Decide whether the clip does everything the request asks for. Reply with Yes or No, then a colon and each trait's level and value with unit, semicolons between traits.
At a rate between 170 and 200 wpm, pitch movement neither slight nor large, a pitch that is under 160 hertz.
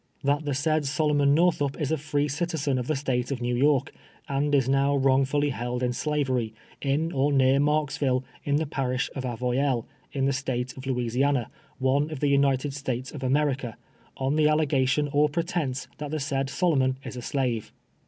No: average, 190 wpm; narrow, 2.1 semitones; medium, 140 Hz